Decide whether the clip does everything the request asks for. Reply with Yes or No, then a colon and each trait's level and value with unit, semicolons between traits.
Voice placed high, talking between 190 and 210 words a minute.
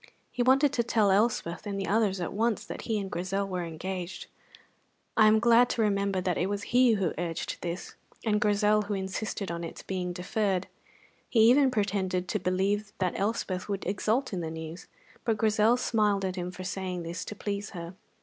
Yes: high, 200 Hz; average, 195 wpm